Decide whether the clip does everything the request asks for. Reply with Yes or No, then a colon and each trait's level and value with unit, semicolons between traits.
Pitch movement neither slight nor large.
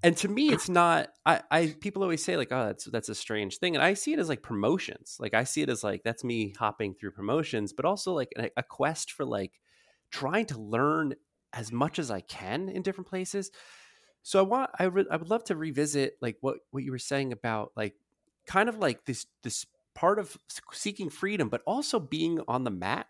No: wide, 8.5 semitones